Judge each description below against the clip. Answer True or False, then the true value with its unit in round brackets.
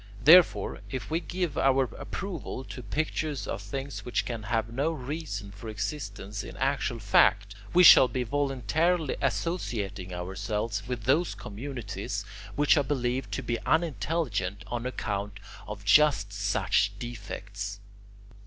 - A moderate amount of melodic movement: False (6.0 semitones)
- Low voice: True (120 Hz)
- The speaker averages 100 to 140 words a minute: True (135 wpm)